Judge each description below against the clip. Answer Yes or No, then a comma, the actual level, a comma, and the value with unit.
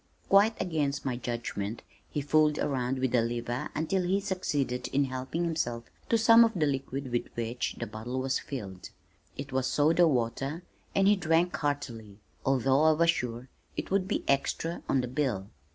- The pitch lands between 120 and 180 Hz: Yes, low, 135 Hz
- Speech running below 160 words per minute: No, average, 175 wpm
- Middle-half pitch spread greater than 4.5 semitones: Yes, average, 5.0 semitones